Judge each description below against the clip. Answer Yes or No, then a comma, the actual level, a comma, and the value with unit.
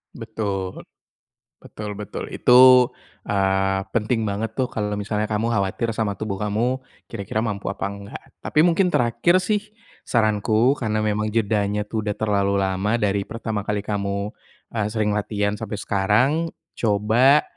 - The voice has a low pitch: Yes, low, 105 Hz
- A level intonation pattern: Yes, narrow, 2.1 semitones